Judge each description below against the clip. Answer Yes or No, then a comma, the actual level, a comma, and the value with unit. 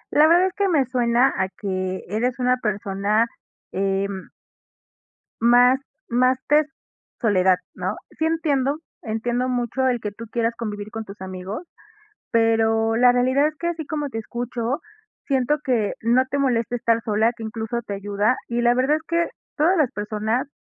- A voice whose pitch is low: No, high, 235 Hz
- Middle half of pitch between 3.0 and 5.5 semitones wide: Yes, average, 3.5 semitones